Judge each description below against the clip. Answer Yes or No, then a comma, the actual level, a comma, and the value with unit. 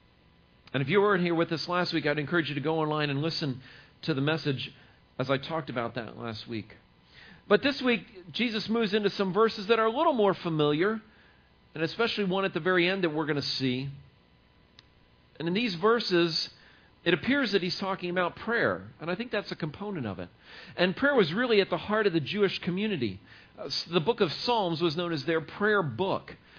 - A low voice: No, medium, 170 Hz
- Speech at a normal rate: No, fast, 215 wpm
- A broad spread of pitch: Yes, wide, 6.4 semitones